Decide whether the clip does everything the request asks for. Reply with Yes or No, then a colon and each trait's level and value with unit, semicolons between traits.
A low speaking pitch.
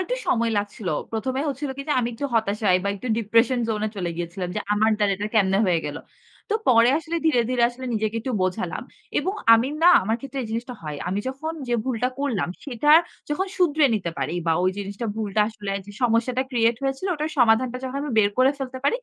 No: high, 230 Hz